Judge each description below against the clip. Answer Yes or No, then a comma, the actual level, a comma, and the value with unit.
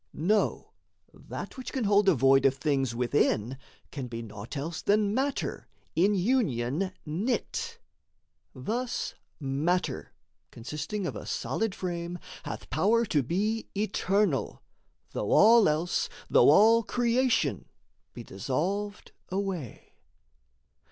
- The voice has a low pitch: No, medium, 180 Hz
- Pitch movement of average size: No, wide, 7.7 semitones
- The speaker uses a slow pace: Yes, slow, 115 wpm